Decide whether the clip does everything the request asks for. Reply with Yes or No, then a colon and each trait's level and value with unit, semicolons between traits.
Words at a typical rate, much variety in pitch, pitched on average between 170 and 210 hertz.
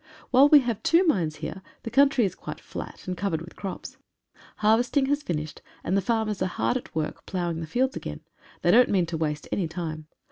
No: fast, 210 wpm; wide, 7.0 semitones; high, 190 Hz